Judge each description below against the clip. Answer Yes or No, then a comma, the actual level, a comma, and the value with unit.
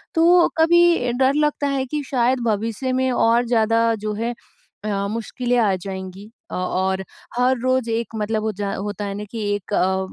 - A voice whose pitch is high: Yes, high, 230 Hz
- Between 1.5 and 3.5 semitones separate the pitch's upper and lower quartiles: No, average, 4.1 semitones